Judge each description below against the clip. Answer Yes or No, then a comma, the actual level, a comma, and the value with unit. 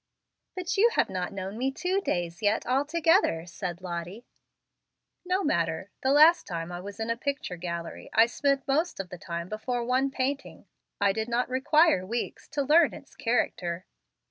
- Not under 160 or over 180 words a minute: Yes, average, 170 wpm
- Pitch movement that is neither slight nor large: No, wide, 7.8 semitones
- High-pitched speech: Yes, high, 235 Hz